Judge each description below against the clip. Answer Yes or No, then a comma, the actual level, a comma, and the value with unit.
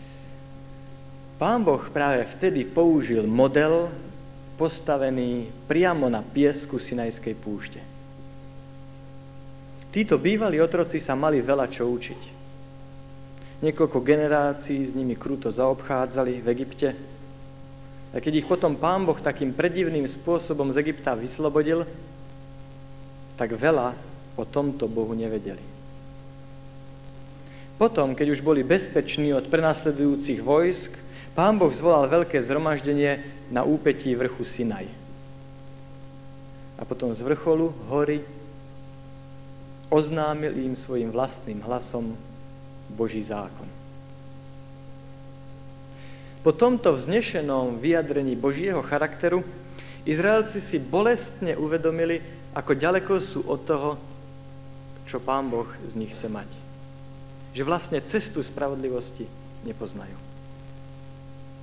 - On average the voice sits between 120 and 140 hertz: Yes, low, 135 Hz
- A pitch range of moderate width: No, narrow, 1.9 semitones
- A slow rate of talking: Yes, slow, 100 wpm